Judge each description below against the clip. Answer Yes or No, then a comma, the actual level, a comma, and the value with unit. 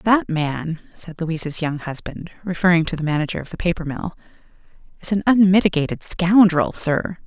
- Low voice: No, medium, 170 Hz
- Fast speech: No, average, 155 wpm